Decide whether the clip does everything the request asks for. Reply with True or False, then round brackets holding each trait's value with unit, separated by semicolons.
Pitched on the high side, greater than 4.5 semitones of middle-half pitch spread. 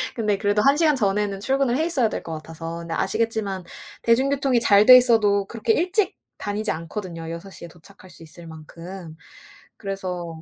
True (200 Hz; 5.6 semitones)